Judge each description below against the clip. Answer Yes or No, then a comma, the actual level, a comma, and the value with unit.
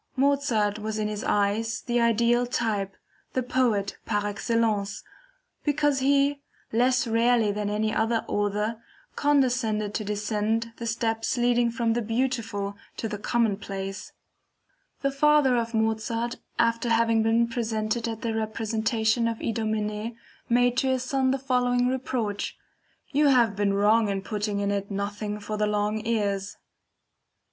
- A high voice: Yes, high, 225 Hz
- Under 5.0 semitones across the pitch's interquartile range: Yes, narrow, 2.6 semitones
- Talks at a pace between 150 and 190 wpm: No, average, 140 wpm